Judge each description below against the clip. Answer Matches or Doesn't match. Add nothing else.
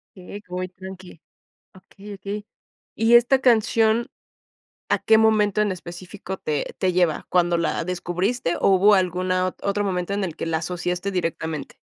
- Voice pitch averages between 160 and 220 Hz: Matches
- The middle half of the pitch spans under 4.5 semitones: Matches